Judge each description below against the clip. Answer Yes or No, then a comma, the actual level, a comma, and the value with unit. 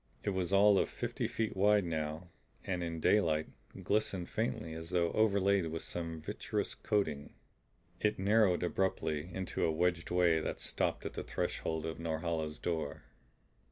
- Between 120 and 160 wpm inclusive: Yes, average, 155 wpm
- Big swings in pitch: No, average, 3.5 semitones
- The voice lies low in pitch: Yes, very low, 85 Hz